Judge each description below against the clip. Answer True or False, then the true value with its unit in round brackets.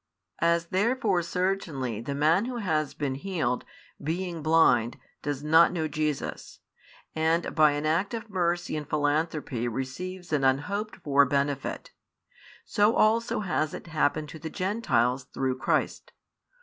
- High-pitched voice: False (155 Hz)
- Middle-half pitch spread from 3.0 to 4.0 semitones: False (4.4 semitones)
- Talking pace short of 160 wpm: True (140 wpm)